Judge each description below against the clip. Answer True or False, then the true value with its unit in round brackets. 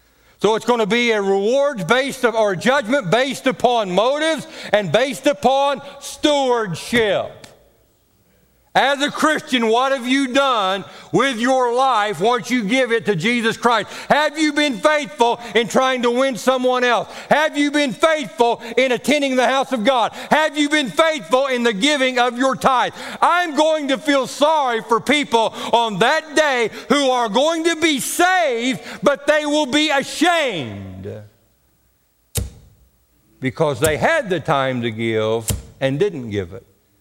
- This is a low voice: False (245 Hz)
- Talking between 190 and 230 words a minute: False (155 wpm)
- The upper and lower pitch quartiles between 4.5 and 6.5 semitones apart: True (5.2 semitones)